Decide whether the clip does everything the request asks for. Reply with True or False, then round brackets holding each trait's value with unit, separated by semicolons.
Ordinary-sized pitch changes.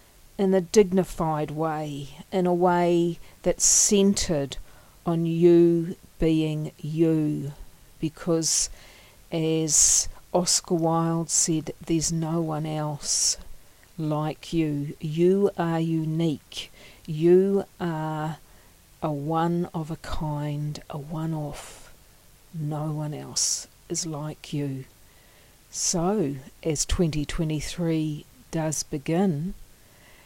False (2.3 semitones)